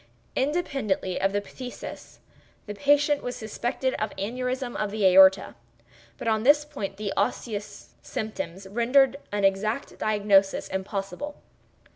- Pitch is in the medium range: No, high, 215 Hz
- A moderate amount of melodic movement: Yes, average, 4.9 semitones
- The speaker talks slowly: Yes, slow, 125 wpm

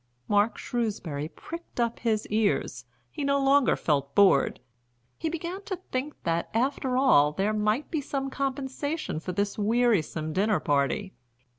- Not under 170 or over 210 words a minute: No, average, 145 wpm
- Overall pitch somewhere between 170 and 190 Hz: No, high, 225 Hz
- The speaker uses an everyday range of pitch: No, wide, 6.8 semitones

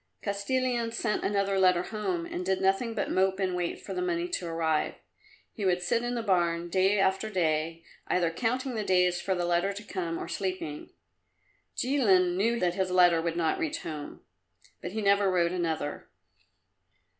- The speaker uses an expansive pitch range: No, average, 3.4 semitones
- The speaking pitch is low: No, high, 190 Hz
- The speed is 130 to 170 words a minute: No, average, 180 wpm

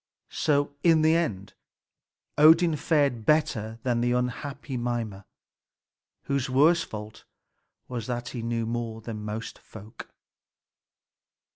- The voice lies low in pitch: Yes, low, 125 Hz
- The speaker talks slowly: Yes, slow, 115 wpm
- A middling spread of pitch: Yes, average, 4.6 semitones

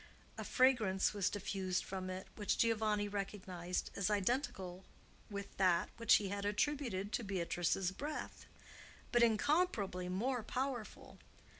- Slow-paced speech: Yes, slow, 125 wpm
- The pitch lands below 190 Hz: No, high, 205 Hz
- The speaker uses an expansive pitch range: No, average, 3.7 semitones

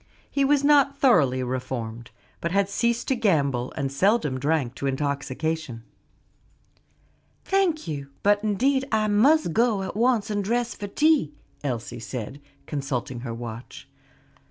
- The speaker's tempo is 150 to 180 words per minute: No, slow, 135 wpm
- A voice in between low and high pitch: Yes, medium, 170 Hz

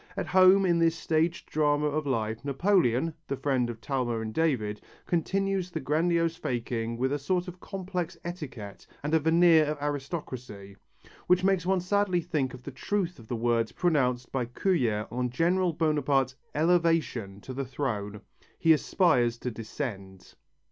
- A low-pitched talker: No, medium, 145 Hz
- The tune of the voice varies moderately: No, wide, 6.1 semitones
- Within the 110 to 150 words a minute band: No, average, 160 wpm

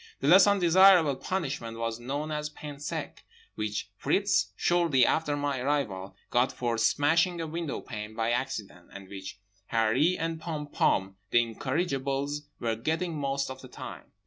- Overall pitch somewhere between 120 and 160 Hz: Yes, medium, 140 Hz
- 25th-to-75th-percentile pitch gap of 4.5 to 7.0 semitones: Yes, wide, 5.6 semitones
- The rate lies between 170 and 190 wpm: No, average, 150 wpm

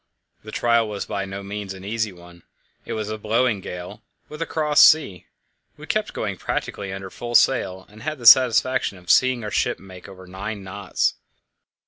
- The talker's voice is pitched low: Yes, low, 105 Hz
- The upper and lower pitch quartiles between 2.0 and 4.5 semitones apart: Yes, average, 3.8 semitones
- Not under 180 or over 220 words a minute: Yes, average, 185 wpm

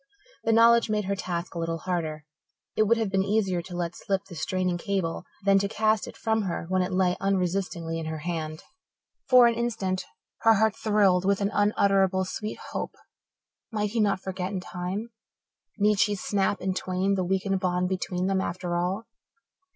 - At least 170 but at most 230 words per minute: Yes, average, 185 wpm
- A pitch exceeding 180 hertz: Yes, high, 190 Hz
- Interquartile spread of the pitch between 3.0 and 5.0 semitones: No, narrow, 2.4 semitones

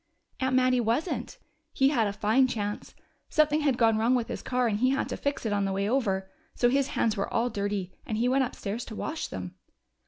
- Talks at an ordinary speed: No, fast, 225 wpm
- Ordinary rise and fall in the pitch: Yes, average, 4.1 semitones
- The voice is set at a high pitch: Yes, high, 235 Hz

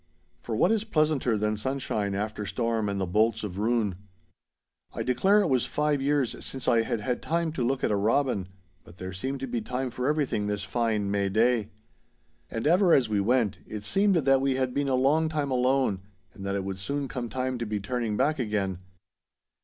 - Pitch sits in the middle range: No, low, 120 Hz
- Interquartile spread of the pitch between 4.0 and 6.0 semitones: Yes, average, 4.6 semitones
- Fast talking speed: Yes, fast, 210 wpm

